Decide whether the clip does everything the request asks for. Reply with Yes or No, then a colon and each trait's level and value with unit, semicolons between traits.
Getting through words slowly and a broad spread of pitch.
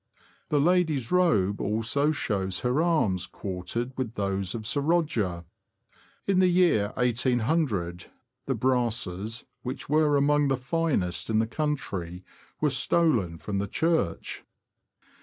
Yes: slow, 125 wpm; wide, 7.3 semitones